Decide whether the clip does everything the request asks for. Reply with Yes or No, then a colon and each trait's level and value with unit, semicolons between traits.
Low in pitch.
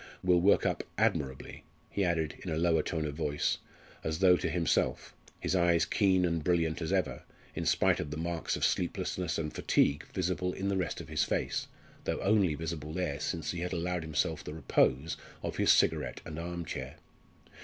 Yes: very low, 85 Hz